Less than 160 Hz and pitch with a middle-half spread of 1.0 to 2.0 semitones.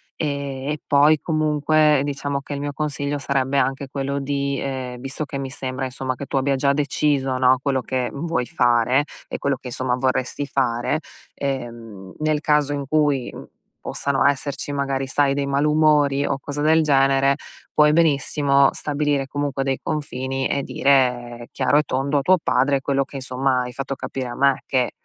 Yes: medium, 140 Hz; narrow, 1.6 semitones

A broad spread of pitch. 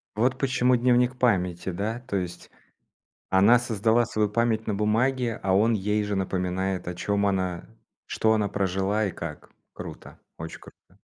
No: average, 3.6 semitones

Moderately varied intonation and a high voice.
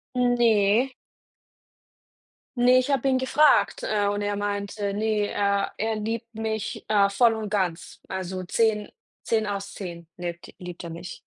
No: narrow, 2.3 semitones; high, 205 Hz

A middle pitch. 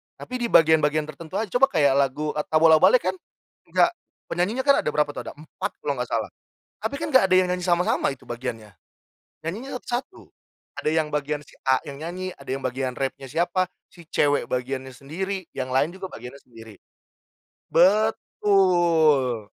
Yes: medium, 155 Hz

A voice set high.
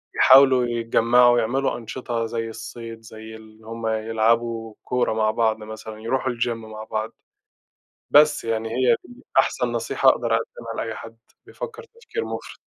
No: low, 115 Hz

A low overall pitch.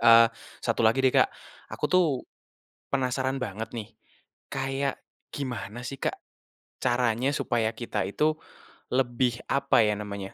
Yes: low, 125 Hz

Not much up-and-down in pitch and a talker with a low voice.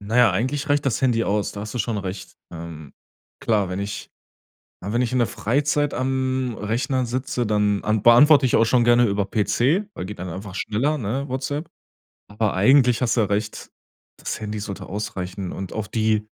No: average, 4.1 semitones; low, 110 Hz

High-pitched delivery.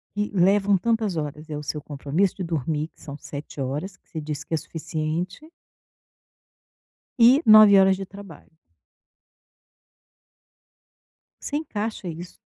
No: medium, 175 Hz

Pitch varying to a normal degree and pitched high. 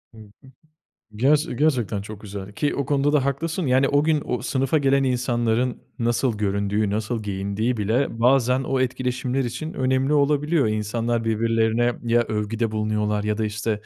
No: average, 4.0 semitones; low, 120 Hz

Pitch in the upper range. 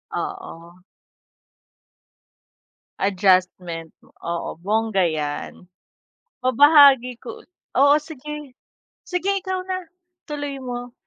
Yes: high, 245 Hz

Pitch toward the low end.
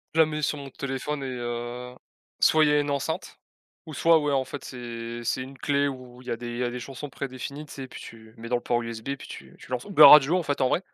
Yes: low, 130 Hz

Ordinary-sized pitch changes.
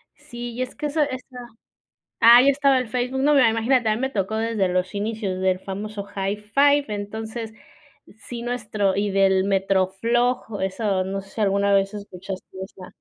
Yes: average, 4.0 semitones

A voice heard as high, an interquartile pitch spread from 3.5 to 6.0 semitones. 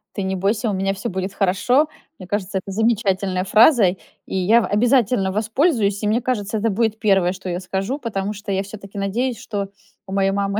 No: high, 200 Hz; average, 2.7 semitones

